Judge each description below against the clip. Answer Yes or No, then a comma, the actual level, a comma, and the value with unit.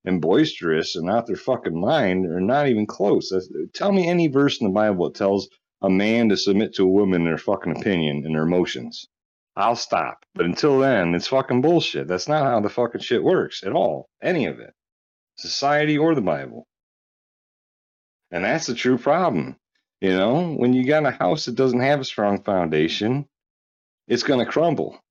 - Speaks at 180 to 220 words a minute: Yes, average, 195 wpm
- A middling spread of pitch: No, wide, 7.1 semitones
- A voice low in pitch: Yes, low, 110 Hz